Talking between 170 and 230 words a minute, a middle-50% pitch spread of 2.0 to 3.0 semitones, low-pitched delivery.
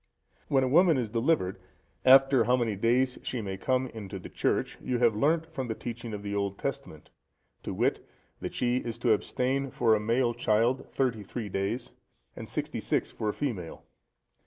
No: average, 185 wpm; average, 3.6 semitones; low, 120 Hz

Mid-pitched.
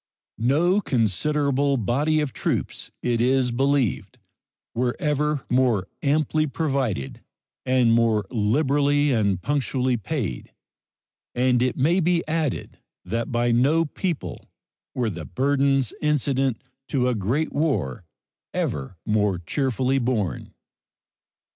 No: low, 130 Hz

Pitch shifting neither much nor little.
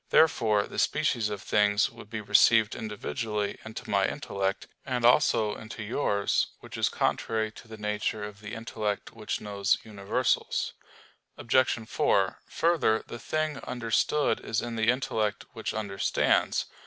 No: narrow, 2.1 semitones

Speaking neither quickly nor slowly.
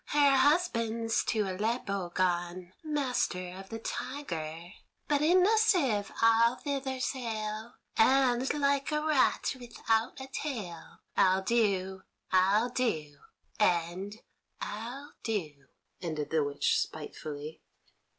No: slow, 110 wpm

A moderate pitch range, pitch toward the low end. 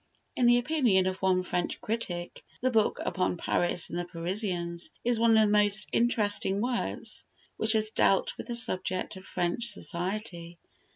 No: average, 4.4 semitones; high, 205 Hz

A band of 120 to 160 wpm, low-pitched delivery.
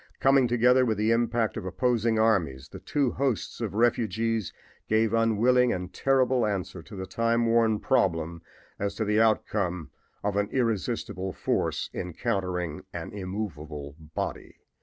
Yes: average, 140 wpm; low, 110 Hz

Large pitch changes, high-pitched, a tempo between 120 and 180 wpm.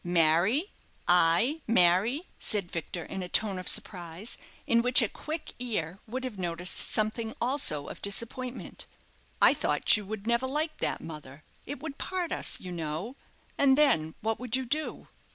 Yes: wide, 6.7 semitones; high, 220 Hz; average, 165 wpm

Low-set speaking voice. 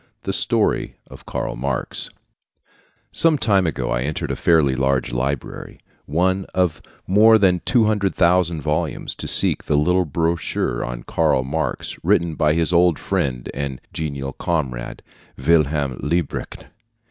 Yes: very low, 80 Hz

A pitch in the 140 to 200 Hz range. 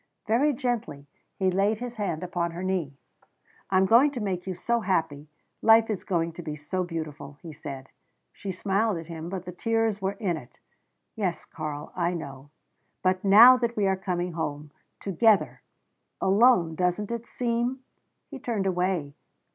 Yes: medium, 185 Hz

